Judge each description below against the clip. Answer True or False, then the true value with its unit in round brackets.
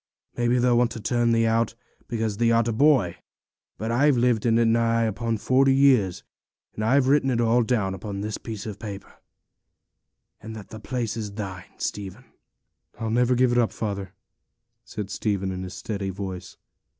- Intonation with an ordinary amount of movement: True (3.0 semitones)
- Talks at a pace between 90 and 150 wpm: False (180 wpm)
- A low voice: True (115 Hz)